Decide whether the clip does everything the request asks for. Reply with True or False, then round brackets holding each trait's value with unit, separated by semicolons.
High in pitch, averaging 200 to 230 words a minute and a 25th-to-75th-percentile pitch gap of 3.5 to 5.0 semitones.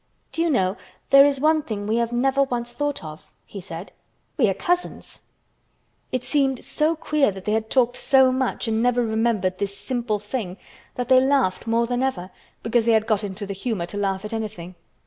True (230 Hz; 205 wpm; 4.5 semitones)